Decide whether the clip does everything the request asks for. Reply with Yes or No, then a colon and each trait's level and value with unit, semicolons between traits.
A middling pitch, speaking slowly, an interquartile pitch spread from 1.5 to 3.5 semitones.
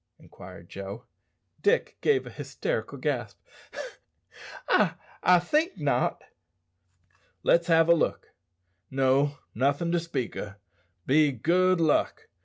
No: medium, 160 Hz; slow, 110 wpm; average, 4.9 semitones